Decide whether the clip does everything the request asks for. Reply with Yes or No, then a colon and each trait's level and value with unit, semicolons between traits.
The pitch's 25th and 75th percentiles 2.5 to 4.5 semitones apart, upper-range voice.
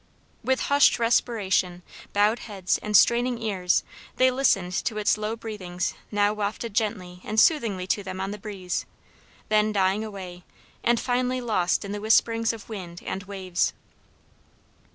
Yes: average, 3.3 semitones; high, 210 Hz